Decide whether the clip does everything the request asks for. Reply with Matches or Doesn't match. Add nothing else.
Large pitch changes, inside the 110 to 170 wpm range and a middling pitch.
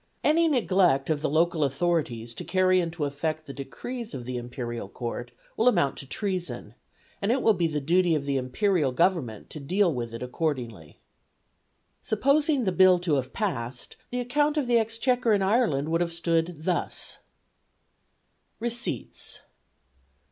Matches